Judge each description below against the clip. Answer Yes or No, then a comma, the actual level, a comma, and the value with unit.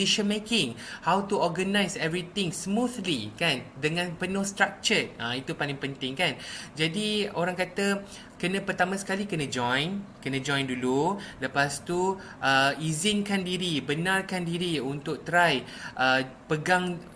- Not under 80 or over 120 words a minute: No, average, 135 wpm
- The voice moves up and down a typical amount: No, wide, 5.7 semitones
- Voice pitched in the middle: Yes, medium, 180 Hz